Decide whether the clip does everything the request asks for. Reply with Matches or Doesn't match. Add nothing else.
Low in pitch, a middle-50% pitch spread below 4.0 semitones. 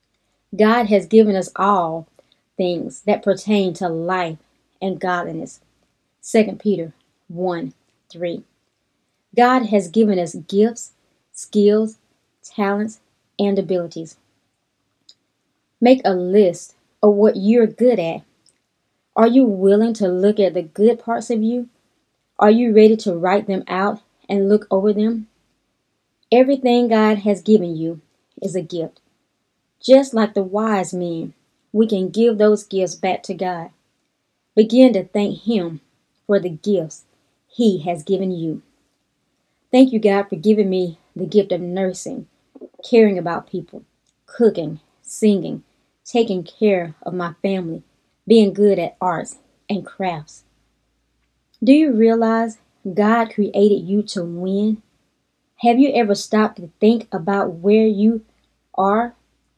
Doesn't match